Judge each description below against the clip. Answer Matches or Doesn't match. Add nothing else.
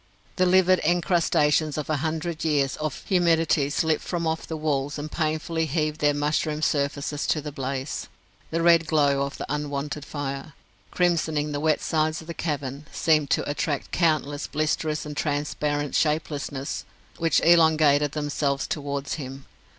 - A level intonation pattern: Matches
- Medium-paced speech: Matches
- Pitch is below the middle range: Doesn't match